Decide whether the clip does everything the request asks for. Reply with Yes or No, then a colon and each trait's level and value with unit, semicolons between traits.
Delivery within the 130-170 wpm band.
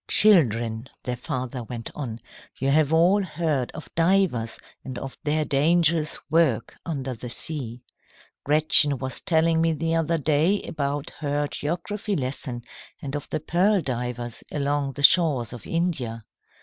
Yes: average, 145 wpm